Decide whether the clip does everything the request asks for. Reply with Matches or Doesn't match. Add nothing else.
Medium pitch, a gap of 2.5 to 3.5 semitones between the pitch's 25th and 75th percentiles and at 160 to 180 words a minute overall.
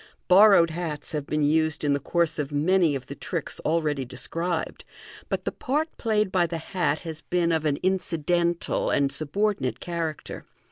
Matches